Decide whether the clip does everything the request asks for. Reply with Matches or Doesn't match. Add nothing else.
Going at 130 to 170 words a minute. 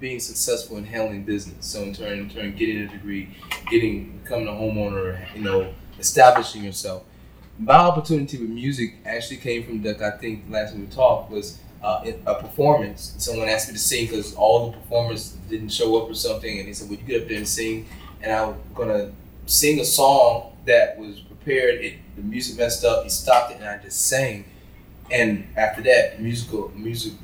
Doesn't match